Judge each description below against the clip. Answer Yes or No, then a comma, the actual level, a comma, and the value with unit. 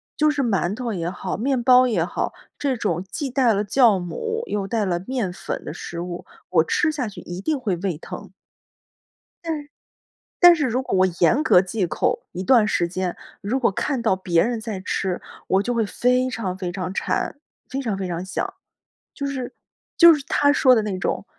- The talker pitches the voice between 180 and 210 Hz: No, high, 220 Hz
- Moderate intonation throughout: No, wide, 5.8 semitones